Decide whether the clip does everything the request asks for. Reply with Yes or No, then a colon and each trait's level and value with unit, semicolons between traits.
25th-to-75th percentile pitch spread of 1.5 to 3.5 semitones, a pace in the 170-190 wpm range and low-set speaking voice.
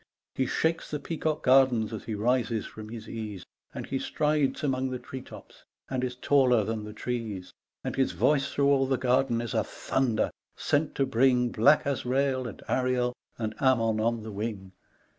Yes: average, 3.2 semitones; average, 180 wpm; low, 125 Hz